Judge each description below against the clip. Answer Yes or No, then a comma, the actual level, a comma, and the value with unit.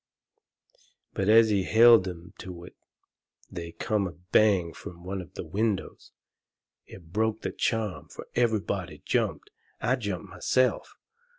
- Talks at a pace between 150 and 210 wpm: No, slow, 135 wpm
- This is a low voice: Yes, low, 100 Hz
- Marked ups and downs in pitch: No, average, 3.9 semitones